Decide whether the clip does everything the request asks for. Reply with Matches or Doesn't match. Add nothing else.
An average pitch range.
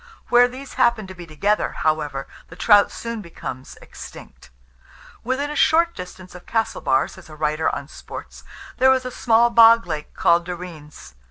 Doesn't match